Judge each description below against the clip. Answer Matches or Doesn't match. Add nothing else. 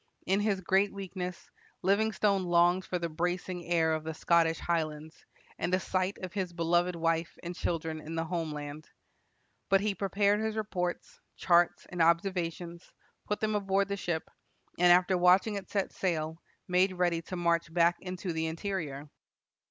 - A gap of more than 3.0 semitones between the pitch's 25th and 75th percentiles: Doesn't match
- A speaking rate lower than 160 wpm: Doesn't match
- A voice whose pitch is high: Doesn't match